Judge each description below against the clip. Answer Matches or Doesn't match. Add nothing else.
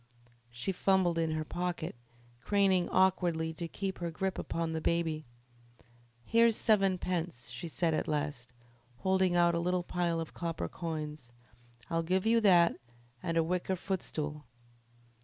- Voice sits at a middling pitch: Matches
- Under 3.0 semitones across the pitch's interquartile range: Matches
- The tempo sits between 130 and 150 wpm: Matches